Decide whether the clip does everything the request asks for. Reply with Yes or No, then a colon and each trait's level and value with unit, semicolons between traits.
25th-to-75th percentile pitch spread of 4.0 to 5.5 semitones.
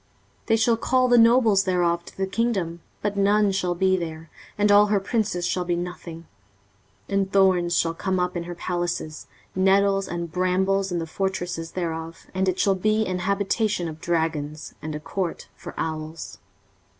No: average, 2.7 semitones